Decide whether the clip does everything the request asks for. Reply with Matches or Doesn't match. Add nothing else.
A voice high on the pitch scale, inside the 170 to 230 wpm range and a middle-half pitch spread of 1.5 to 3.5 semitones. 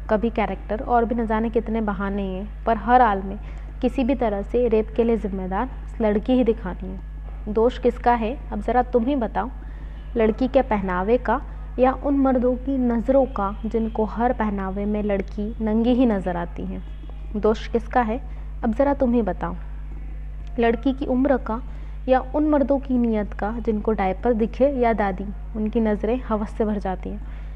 Matches